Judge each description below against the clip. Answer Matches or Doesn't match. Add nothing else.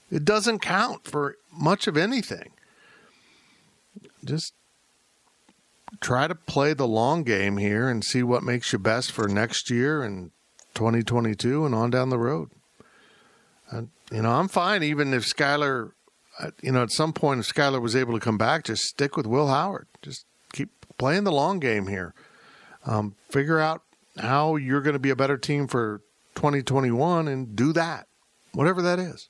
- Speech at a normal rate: Matches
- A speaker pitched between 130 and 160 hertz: Matches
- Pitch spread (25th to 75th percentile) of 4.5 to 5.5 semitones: Matches